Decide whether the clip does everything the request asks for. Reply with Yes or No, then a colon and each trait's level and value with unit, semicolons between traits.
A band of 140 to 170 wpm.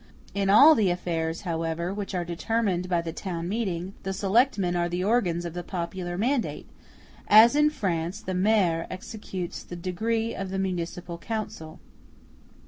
Yes: average, 155 wpm